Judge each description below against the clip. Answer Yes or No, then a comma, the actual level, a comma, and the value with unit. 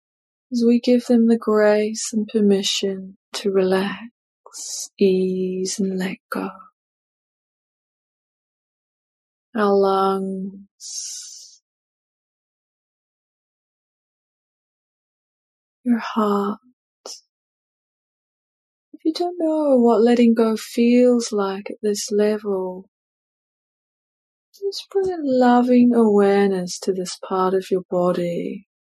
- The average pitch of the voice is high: Yes, high, 210 Hz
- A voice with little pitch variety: No, average, 4.0 semitones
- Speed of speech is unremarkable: No, slow, 85 wpm